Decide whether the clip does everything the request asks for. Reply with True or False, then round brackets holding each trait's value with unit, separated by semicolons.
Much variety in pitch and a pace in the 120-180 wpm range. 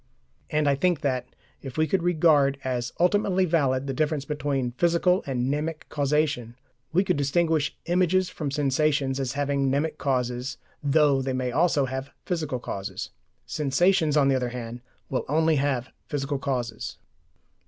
False (3.2 semitones; 155 wpm)